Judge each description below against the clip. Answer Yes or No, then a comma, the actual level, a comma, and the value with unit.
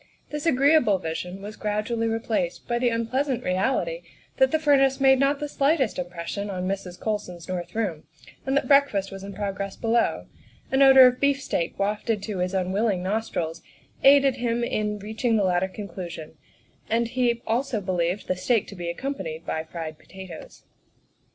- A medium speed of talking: Yes, average, 165 wpm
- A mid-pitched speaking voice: No, high, 210 Hz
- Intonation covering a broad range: Yes, wide, 5.7 semitones